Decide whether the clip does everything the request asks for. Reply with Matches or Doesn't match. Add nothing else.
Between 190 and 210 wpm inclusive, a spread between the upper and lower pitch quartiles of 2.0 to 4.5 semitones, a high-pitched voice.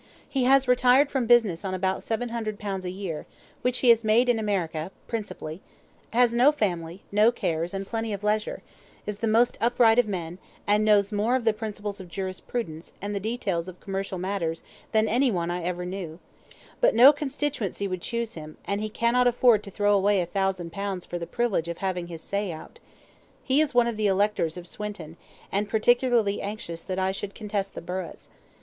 Matches